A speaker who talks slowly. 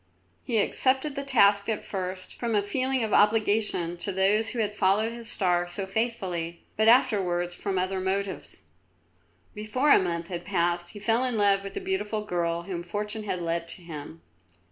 No: average, 185 wpm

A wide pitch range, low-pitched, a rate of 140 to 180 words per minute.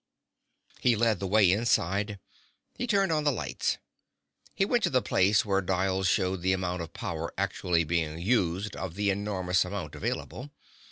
No: average, 3.3 semitones; very low, 95 Hz; average, 160 wpm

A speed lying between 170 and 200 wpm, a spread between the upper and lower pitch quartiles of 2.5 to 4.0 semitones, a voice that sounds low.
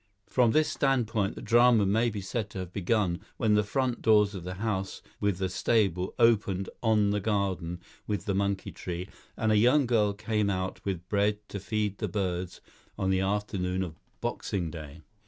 Yes: average, 185 wpm; average, 2.8 semitones; low, 100 Hz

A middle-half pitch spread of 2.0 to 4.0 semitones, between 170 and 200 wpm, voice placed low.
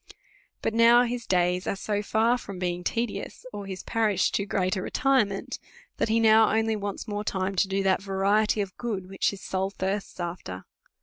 No: average, 2.8 semitones; average, 190 wpm; high, 200 Hz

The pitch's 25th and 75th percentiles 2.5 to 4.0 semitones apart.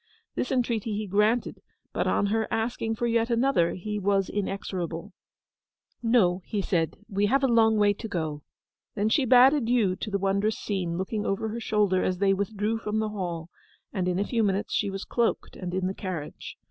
Yes: average, 3.0 semitones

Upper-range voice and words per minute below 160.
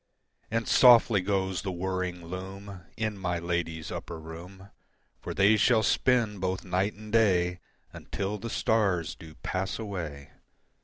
No: very low, 95 Hz; average, 140 wpm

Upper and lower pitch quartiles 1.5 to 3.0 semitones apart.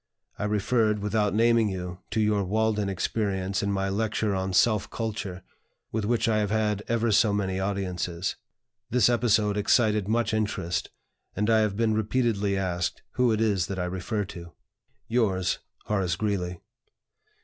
Yes: narrow, 2.4 semitones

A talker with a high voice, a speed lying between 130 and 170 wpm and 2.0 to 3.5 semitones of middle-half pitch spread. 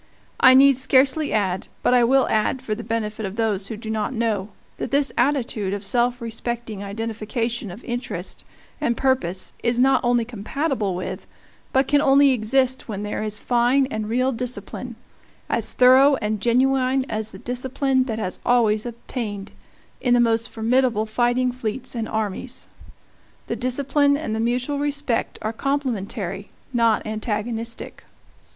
Yes: high, 235 Hz; average, 155 wpm; average, 3.2 semitones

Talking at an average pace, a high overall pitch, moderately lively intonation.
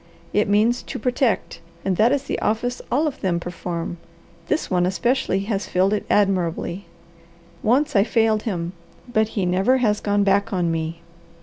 Yes: average, 170 wpm; high, 205 Hz; average, 4.3 semitones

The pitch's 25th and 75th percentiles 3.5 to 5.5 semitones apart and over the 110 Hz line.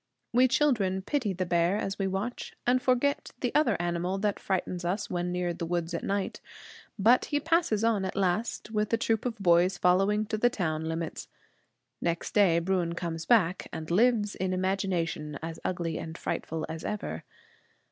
Yes: average, 4.0 semitones; high, 190 Hz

